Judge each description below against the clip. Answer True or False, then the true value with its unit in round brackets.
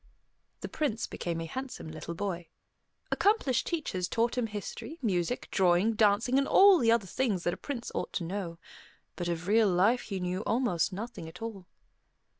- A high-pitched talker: True (205 Hz)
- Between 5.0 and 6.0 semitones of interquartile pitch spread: True (5.3 semitones)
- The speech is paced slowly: False (175 wpm)